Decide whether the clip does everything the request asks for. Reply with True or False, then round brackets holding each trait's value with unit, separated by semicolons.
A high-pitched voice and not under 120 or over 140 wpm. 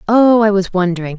False (200 Hz; 205 wpm)